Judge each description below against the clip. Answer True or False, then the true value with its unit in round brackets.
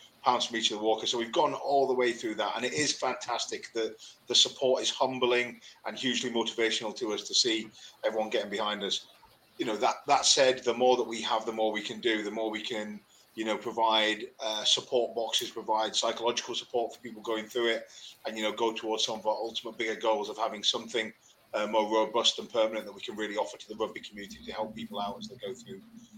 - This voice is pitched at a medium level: False (115 Hz)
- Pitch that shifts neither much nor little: False (1.9 semitones)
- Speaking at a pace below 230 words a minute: False (235 wpm)